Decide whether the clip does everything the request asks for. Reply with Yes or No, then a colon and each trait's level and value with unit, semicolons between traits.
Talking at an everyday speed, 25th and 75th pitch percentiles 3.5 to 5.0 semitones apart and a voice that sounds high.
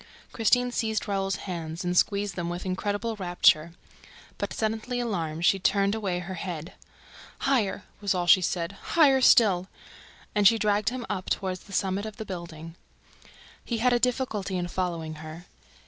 Yes: average, 160 wpm; average, 3.8 semitones; high, 195 Hz